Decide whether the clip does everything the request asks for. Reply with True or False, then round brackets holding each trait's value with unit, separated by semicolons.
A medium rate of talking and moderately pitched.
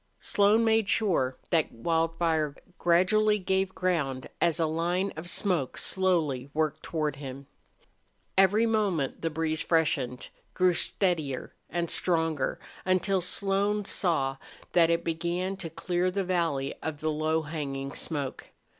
False (130 wpm; 165 Hz)